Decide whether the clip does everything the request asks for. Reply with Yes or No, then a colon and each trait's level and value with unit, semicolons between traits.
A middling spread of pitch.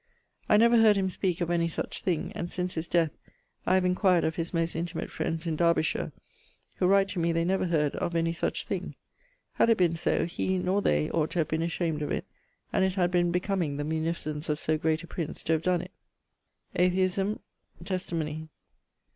No: narrow, 2.3 semitones